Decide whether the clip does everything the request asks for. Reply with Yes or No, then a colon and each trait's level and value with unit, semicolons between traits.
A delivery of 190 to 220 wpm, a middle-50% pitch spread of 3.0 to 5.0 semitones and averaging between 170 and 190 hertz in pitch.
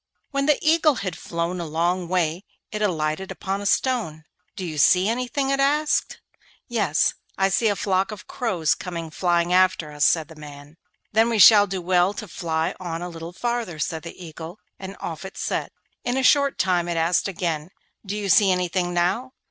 Yes: average, 195 wpm; average, 4.1 semitones; medium, 185 Hz